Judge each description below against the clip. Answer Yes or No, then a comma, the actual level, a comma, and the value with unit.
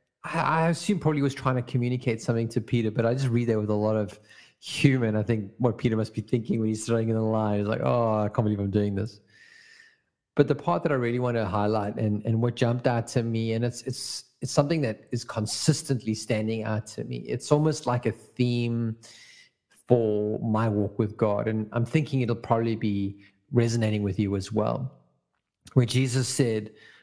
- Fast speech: Yes, fast, 210 wpm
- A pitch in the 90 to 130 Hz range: Yes, low, 115 Hz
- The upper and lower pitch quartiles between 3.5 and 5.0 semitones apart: No, average, 2.7 semitones